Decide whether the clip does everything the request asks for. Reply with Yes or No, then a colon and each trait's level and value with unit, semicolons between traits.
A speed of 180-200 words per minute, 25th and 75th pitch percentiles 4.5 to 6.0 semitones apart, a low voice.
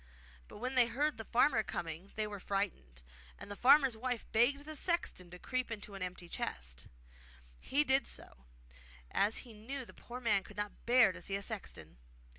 No: average, 195 wpm; average, 4.9 semitones; high, 220 Hz